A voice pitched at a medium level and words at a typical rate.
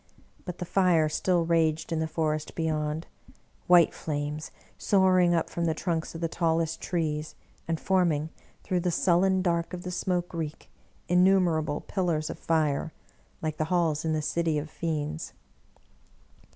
Yes: medium, 165 Hz; average, 165 wpm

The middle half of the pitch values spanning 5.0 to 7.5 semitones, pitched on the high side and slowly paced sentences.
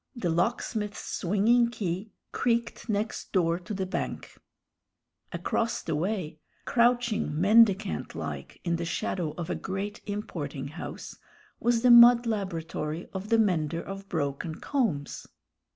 Yes: wide, 5.4 semitones; high, 195 Hz; slow, 130 wpm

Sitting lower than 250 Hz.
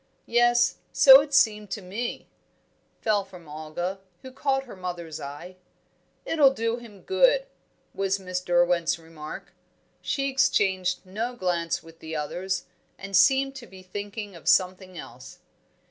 Yes: high, 190 Hz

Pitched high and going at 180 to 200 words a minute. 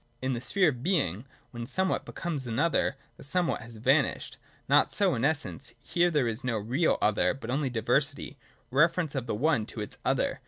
No: low, 135 Hz; average, 190 wpm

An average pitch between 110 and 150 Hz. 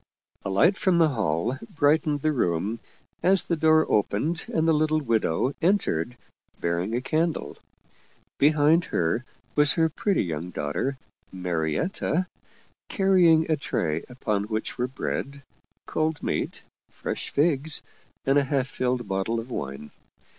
Yes: low, 135 Hz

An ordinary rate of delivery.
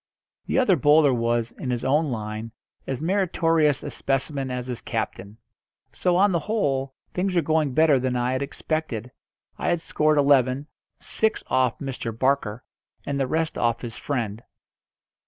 Yes: average, 160 wpm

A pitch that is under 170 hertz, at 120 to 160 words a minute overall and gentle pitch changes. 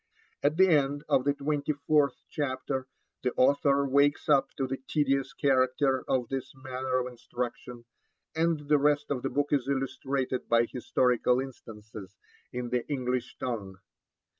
Yes: low, 135 Hz; average, 150 wpm; narrow, 2.2 semitones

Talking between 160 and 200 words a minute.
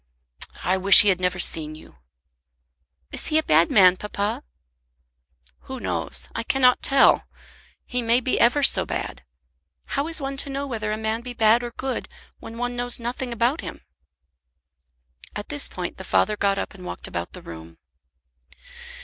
Yes: average, 170 wpm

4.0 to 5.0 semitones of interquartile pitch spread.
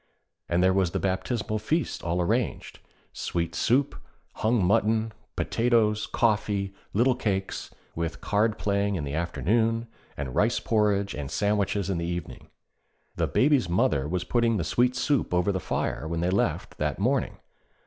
Yes: average, 4.6 semitones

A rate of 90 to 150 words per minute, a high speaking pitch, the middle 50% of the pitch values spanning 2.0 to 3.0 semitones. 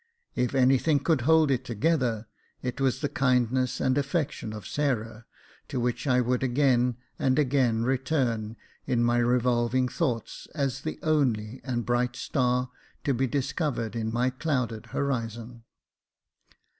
No: average, 145 wpm; low, 125 Hz; narrow, 2.5 semitones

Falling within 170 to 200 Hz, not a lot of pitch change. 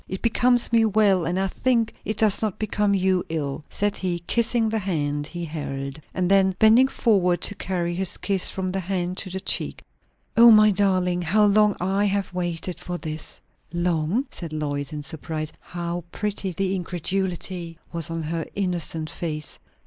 No: medium, 185 Hz; average, 3.4 semitones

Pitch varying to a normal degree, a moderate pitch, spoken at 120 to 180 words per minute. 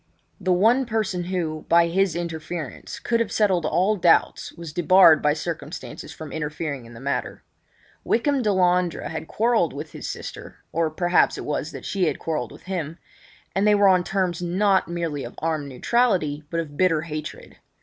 Yes: average, 3.5 semitones; medium, 170 Hz; average, 170 wpm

